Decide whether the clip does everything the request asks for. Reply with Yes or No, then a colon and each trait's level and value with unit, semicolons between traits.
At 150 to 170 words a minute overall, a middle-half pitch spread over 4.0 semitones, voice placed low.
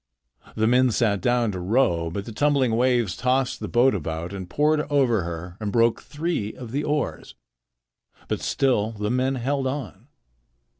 Yes: average, 165 wpm; average, 4.7 semitones; low, 120 Hz